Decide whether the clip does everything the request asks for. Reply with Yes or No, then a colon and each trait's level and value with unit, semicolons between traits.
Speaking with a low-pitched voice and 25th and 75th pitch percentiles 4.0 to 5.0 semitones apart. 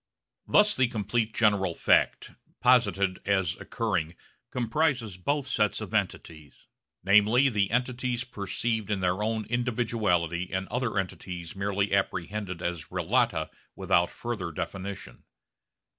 Yes: low, 105 Hz; average, 4.6 semitones